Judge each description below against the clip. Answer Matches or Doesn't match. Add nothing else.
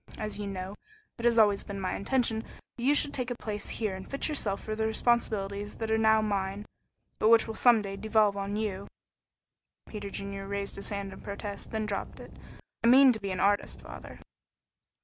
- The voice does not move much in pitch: Matches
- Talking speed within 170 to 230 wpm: Matches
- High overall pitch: Matches